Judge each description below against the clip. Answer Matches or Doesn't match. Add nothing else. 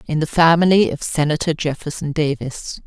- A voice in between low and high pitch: Matches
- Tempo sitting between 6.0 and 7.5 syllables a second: Doesn't match